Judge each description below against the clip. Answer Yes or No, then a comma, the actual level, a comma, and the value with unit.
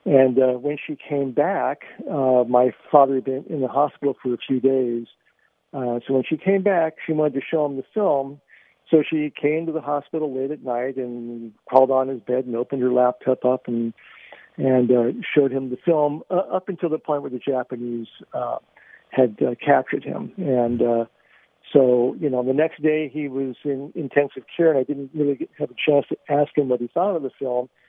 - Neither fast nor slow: No, fast, 215 wpm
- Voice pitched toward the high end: No, low, 135 Hz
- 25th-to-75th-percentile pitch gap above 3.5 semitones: No, average, 2.9 semitones